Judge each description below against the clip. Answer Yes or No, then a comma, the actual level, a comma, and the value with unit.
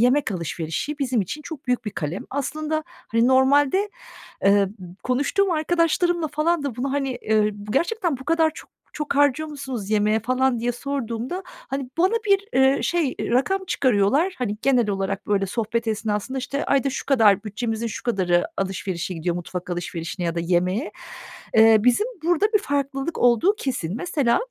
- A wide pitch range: Yes, wide, 6.0 semitones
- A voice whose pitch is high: Yes, very high, 255 Hz